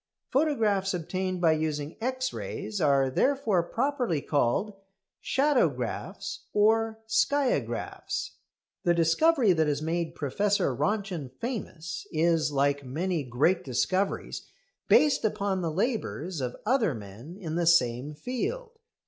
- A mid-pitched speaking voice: Yes, medium, 180 Hz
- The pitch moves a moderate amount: No, wide, 6.6 semitones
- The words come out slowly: Yes, slow, 115 wpm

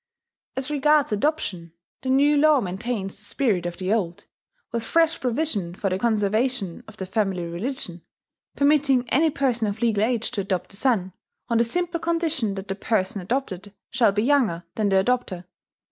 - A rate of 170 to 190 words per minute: Yes, average, 175 wpm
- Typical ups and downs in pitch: No, wide, 5.8 semitones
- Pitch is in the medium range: No, high, 225 Hz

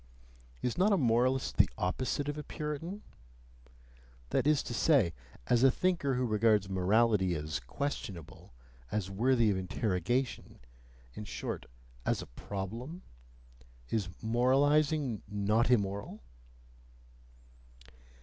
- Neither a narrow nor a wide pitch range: No, wide, 5.9 semitones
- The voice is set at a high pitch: No, low, 120 Hz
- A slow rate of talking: Yes, slow, 110 wpm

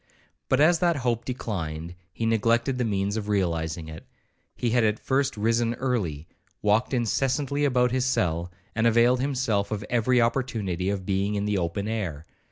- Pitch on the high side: No, low, 110 Hz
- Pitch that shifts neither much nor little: Yes, average, 4.3 semitones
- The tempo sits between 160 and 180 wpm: Yes, average, 170 wpm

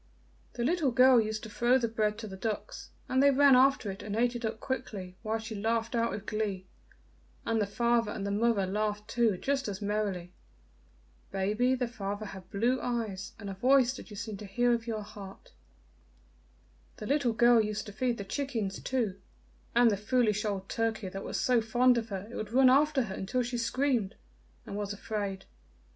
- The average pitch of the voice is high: Yes, high, 220 Hz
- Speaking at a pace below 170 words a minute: No, average, 200 wpm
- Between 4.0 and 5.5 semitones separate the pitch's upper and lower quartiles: No, average, 3.1 semitones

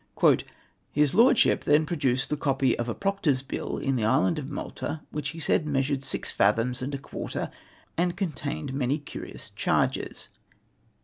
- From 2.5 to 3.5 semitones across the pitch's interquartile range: Yes, average, 3.1 semitones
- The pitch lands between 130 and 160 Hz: Yes, medium, 140 Hz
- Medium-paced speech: Yes, average, 165 wpm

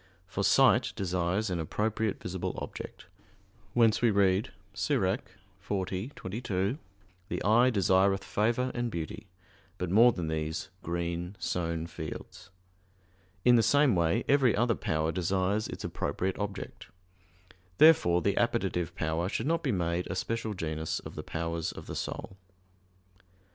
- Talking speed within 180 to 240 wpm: No, slow, 135 wpm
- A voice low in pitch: Yes, very low, 95 Hz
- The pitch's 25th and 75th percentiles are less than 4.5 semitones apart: No, average, 4.8 semitones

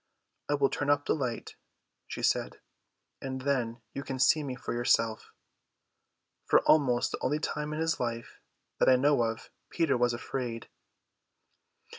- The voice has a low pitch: Yes, low, 130 Hz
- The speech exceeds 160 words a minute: No, average, 150 wpm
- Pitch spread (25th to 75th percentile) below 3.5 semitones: Yes, average, 3.1 semitones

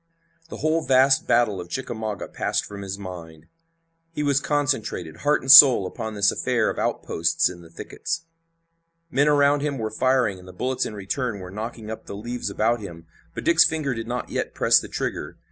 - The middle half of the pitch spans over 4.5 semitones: Yes, wide, 5.6 semitones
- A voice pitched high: No, low, 115 Hz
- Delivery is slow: No, average, 195 wpm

